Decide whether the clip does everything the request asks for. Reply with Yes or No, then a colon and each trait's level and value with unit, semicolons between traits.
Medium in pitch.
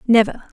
No: high, 225 Hz